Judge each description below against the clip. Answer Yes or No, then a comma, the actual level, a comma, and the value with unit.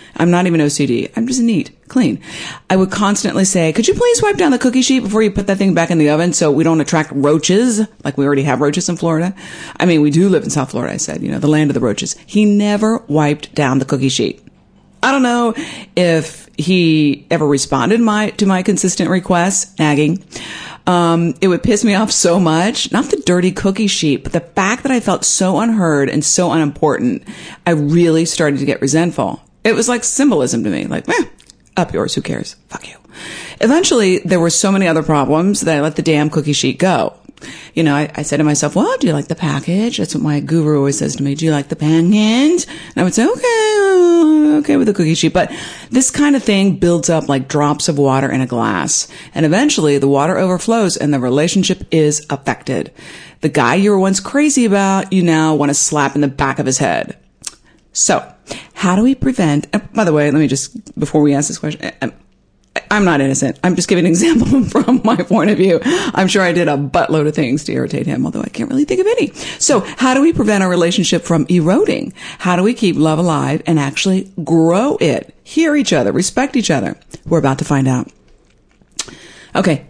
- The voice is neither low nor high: Yes, medium, 175 Hz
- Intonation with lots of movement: Yes, wide, 6.1 semitones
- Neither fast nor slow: No, fast, 220 wpm